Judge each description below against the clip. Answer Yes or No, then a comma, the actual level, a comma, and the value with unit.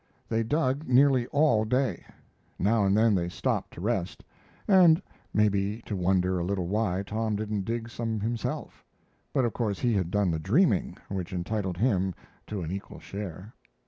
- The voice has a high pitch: No, low, 105 Hz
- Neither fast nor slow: Yes, average, 170 wpm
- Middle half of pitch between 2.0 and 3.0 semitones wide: No, average, 3.7 semitones